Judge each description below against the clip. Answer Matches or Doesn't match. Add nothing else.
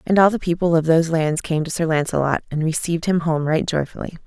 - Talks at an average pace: Doesn't match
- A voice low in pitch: Doesn't match